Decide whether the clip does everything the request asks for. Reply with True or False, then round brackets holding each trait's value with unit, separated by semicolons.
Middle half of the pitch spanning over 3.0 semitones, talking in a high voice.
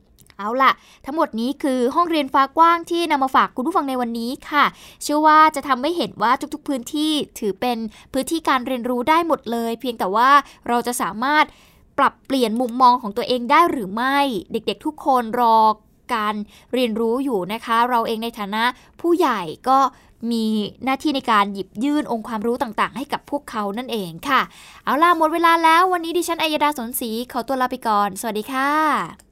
True (4.5 semitones; 255 Hz)